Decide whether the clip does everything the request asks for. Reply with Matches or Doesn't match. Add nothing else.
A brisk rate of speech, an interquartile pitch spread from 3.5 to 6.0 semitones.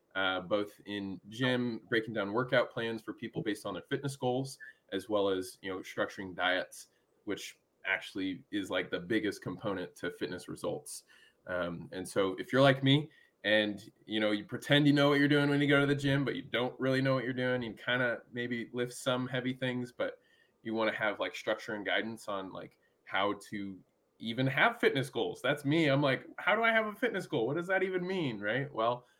Matches